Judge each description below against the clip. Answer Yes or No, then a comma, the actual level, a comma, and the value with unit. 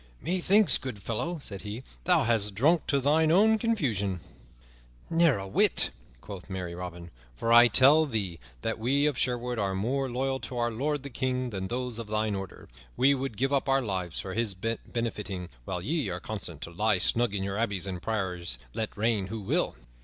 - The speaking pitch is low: Yes, low, 115 Hz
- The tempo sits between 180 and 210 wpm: Yes, average, 190 wpm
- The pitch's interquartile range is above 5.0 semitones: Yes, wide, 5.6 semitones